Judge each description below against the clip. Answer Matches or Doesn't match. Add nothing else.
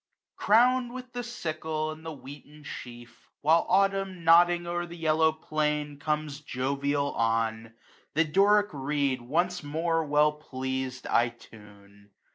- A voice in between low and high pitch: Matches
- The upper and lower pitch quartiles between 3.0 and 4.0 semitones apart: Doesn't match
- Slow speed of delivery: Matches